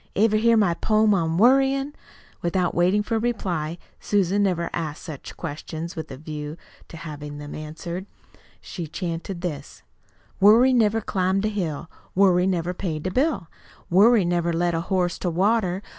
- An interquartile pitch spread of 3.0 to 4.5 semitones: Yes, average, 4.1 semitones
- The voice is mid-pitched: Yes, medium, 180 Hz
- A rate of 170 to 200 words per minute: No, average, 160 wpm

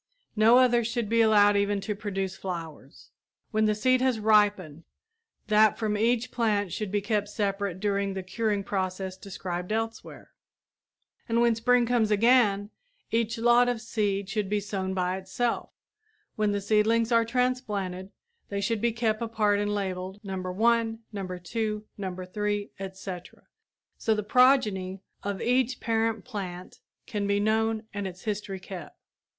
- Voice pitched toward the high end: Yes, high, 210 Hz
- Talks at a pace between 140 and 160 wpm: Yes, average, 155 wpm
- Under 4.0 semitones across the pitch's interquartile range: Yes, average, 2.7 semitones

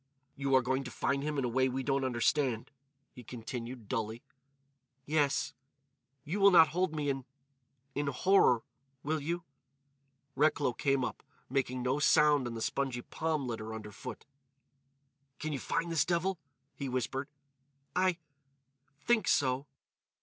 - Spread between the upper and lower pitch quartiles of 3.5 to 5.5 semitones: No, average, 2.9 semitones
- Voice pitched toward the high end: No, low, 135 Hz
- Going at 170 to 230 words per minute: No, slow, 135 wpm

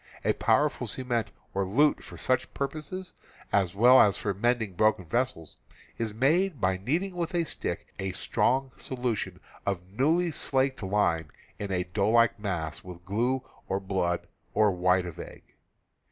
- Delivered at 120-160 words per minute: Yes, average, 155 wpm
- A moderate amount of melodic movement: No, wide, 5.8 semitones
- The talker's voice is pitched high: No, low, 110 Hz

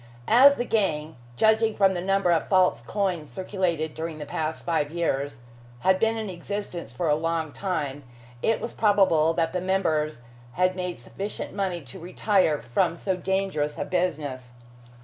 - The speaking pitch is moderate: Yes, medium, 175 Hz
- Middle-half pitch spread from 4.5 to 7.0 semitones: No, average, 4.0 semitones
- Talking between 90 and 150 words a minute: No, average, 165 wpm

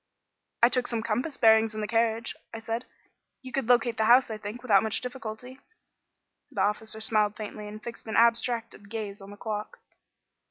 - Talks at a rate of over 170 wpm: Yes, average, 185 wpm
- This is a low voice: No, high, 225 Hz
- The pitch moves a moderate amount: No, narrow, 1.9 semitones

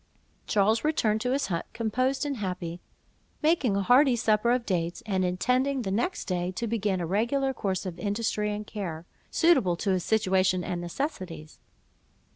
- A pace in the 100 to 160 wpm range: No, average, 170 wpm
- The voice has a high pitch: Yes, high, 210 Hz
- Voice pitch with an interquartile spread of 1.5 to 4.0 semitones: No, average, 5.2 semitones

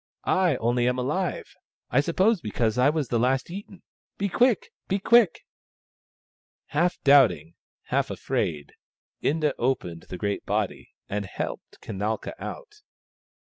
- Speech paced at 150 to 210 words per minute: No, slow, 135 wpm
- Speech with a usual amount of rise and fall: No, wide, 8.6 semitones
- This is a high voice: No, low, 135 Hz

